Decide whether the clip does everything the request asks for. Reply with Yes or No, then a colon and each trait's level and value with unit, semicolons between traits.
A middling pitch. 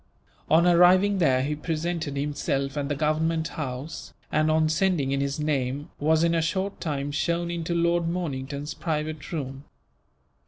Yes: medium, 155 Hz